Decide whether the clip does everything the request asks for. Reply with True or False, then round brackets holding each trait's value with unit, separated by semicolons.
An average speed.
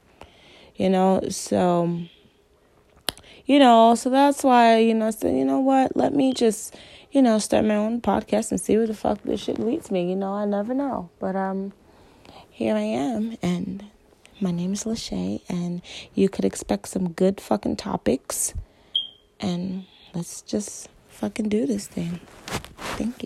True (165 wpm)